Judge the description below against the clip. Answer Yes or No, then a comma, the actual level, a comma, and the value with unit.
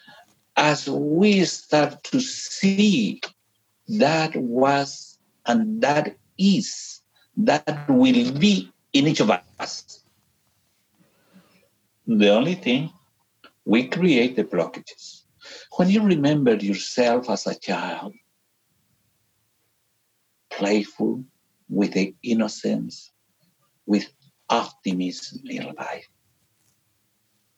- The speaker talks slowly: Yes, slow, 85 wpm